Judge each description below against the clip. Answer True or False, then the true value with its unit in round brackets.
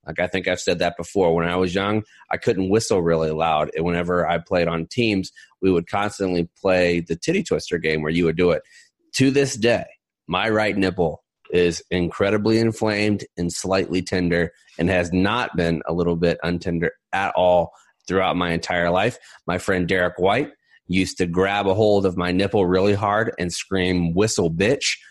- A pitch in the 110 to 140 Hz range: False (90 Hz)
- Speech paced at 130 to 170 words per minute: False (190 wpm)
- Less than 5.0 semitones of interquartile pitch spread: True (2.8 semitones)